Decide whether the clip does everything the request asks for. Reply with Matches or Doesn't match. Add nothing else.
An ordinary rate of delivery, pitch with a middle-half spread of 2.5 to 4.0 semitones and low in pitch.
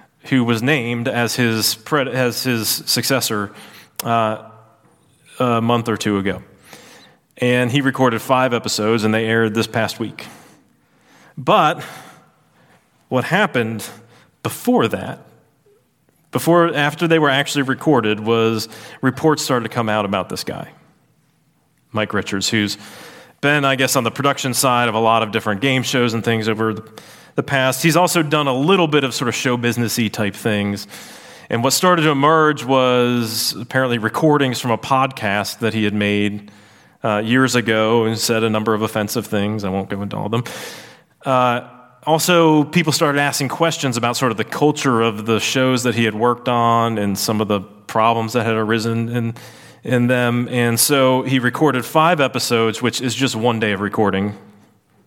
Matches